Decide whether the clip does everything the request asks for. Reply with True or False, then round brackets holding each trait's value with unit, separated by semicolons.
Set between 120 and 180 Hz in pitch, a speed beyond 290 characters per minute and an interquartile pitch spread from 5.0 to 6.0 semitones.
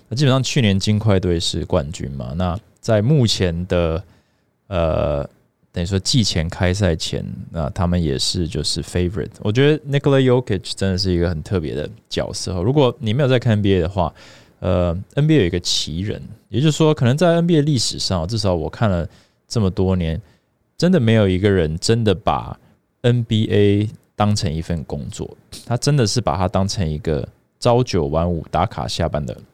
False (100 Hz; 300 characters per minute; 5.5 semitones)